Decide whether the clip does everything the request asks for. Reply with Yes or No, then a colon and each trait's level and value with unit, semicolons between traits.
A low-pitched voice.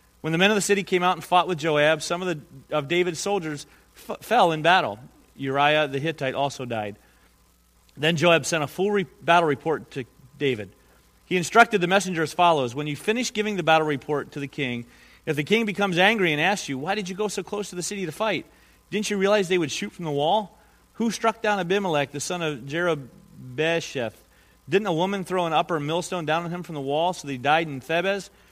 No: medium, 165 Hz